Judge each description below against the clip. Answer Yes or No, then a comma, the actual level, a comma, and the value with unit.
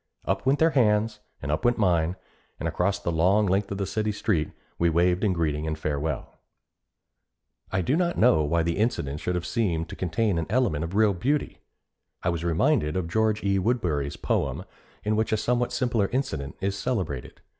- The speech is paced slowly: No, average, 190 wpm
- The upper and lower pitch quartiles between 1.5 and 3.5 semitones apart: No, average, 5.1 semitones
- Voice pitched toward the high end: No, very low, 95 Hz